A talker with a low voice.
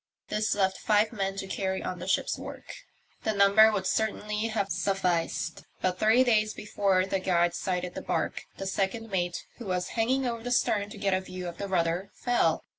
No: high, 195 Hz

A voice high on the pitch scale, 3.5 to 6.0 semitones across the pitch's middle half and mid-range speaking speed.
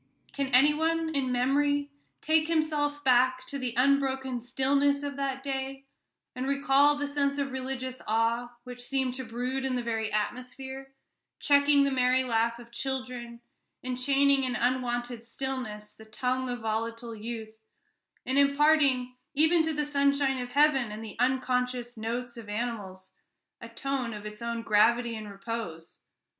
No: very high, 255 Hz; average, 2.9 semitones; average, 155 wpm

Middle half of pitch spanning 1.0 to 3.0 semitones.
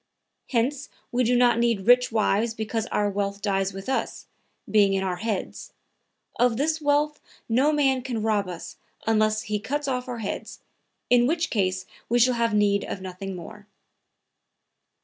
No: average, 3.8 semitones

